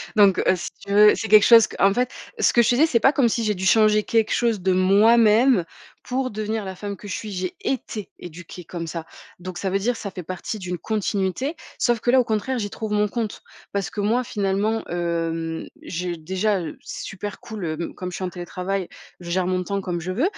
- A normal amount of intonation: Yes, average, 3.5 semitones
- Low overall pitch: No, high, 200 Hz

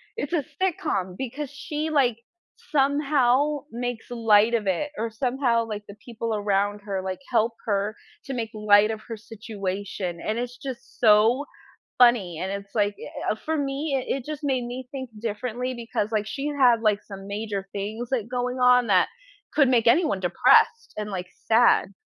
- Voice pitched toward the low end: No, high, 230 Hz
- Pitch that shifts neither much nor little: Yes, average, 4.0 semitones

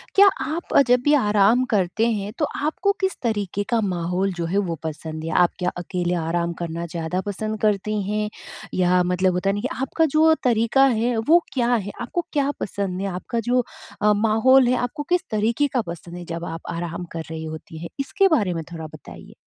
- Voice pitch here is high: Yes, high, 205 Hz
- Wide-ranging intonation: Yes, wide, 5.9 semitones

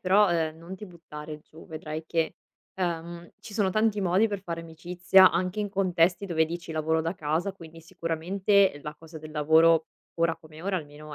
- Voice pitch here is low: No, medium, 165 Hz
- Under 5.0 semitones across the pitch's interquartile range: Yes, average, 2.8 semitones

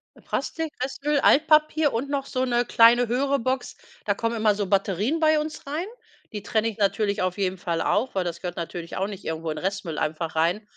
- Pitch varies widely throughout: Yes, wide, 6.8 semitones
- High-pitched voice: Yes, high, 215 Hz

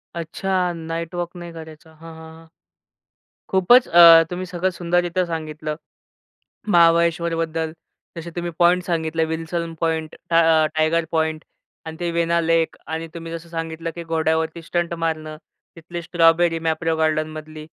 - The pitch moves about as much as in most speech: No, narrow, 1.1 semitones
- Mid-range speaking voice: Yes, medium, 165 Hz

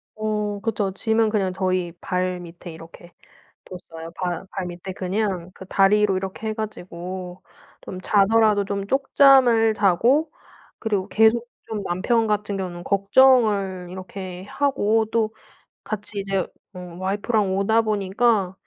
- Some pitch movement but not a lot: Yes, average, 3.0 semitones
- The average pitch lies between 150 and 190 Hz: No, high, 200 Hz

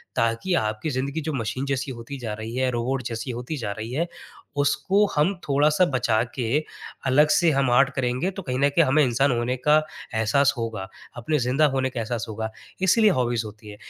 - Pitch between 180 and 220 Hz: No, low, 130 Hz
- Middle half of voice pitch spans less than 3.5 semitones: No, average, 4.0 semitones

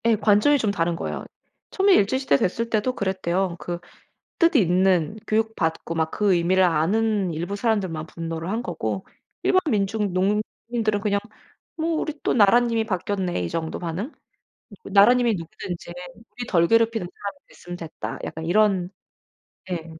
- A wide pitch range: No, average, 4.4 semitones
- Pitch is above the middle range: Yes, high, 200 Hz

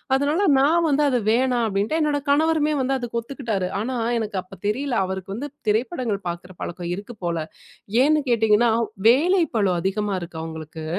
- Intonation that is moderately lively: No, wide, 6.8 semitones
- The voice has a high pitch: Yes, high, 230 Hz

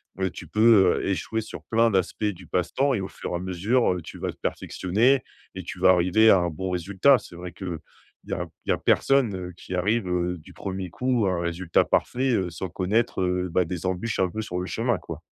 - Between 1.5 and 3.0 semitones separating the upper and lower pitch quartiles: No, average, 3.8 semitones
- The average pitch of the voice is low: Yes, very low, 95 Hz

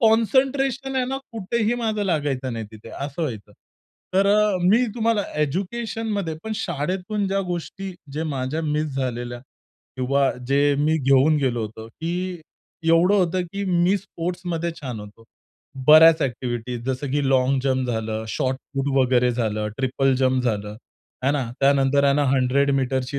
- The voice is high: No, medium, 145 Hz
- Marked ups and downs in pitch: Yes, wide, 6.6 semitones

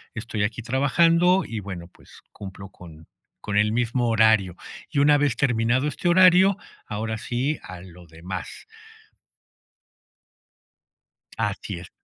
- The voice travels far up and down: Yes, wide, 6.5 semitones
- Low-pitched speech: Yes, low, 115 Hz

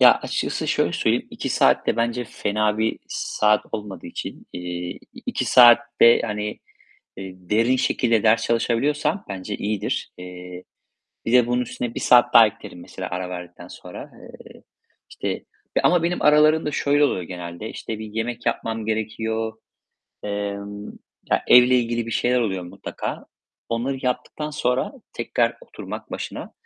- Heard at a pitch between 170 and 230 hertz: No, low, 110 Hz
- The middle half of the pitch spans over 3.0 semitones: Yes, average, 3.4 semitones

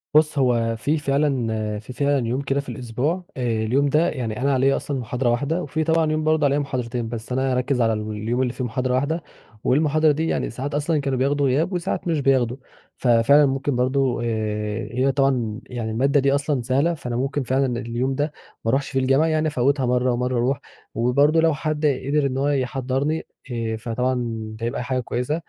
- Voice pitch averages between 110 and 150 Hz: Yes, low, 135 Hz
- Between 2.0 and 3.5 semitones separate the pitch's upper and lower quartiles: Yes, average, 2.9 semitones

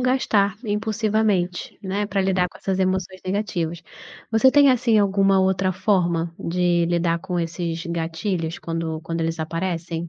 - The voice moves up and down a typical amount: Yes, average, 3.2 semitones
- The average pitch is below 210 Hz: Yes, medium, 185 Hz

